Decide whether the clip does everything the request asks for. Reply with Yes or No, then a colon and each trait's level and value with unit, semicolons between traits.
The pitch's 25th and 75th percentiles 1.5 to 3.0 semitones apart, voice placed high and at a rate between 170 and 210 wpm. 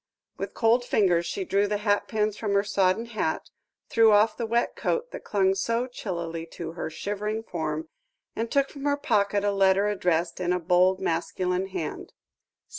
No: average, 3.7 semitones; high, 200 Hz; average, 175 wpm